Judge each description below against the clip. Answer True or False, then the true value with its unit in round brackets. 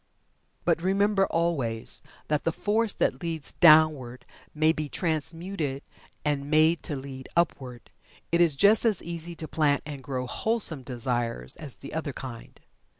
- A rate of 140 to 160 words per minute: True (150 wpm)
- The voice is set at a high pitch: False (155 Hz)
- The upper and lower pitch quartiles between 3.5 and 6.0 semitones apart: True (4.1 semitones)